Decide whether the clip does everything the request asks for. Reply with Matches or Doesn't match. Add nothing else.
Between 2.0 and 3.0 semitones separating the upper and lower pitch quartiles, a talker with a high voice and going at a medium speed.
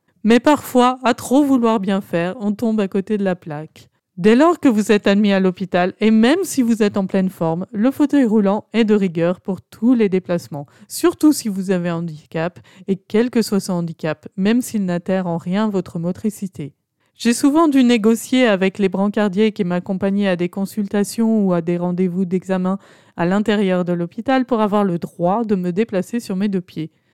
Doesn't match